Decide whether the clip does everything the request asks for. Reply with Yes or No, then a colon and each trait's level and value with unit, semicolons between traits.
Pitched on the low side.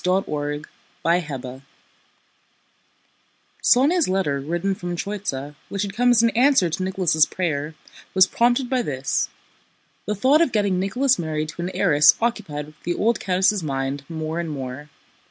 No: medium, 180 Hz